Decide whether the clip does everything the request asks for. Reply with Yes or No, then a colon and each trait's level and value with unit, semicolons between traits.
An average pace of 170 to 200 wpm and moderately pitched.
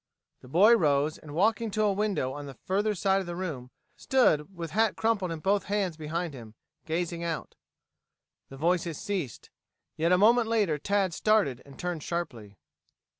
Yes: average, 175 wpm; medium, 175 Hz